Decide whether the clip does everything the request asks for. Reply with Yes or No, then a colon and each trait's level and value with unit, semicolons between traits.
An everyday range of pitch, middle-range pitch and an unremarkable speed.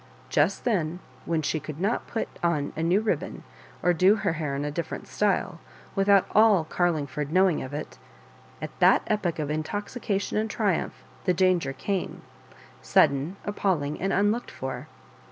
Yes: average, 4.9 semitones; medium, 175 Hz; average, 165 wpm